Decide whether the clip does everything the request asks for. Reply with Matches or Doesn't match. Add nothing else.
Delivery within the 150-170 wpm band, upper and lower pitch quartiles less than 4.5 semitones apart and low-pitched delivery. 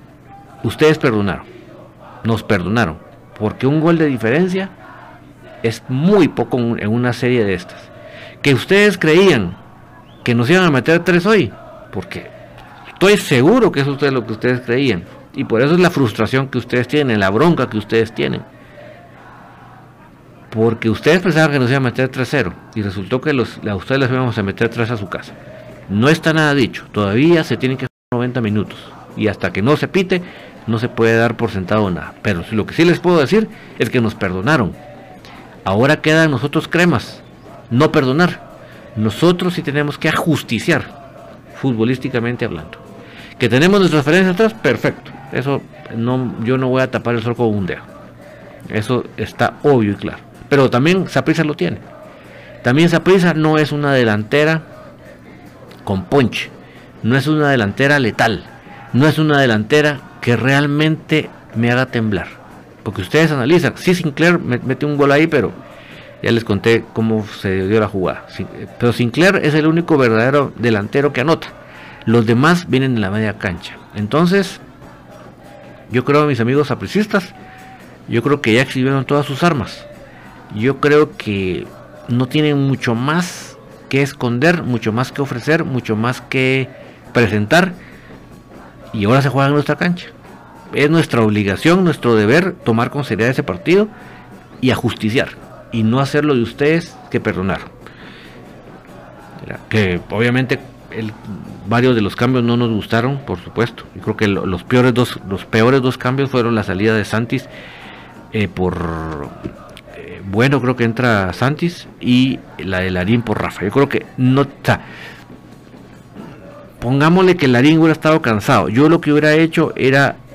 Doesn't match